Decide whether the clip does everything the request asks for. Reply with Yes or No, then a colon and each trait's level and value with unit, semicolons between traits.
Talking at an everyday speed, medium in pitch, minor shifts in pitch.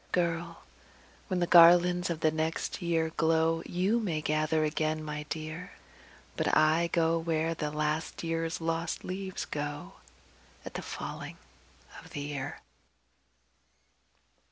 No: slow, 125 wpm; medium, 165 Hz; narrow, 1.7 semitones